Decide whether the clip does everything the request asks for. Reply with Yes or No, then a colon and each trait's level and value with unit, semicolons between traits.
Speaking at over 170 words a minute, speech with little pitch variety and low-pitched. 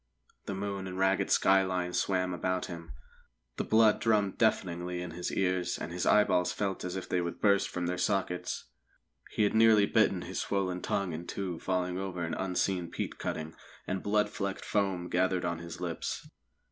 Yes: average, 180 wpm; narrow, 1.8 semitones; very low, 95 Hz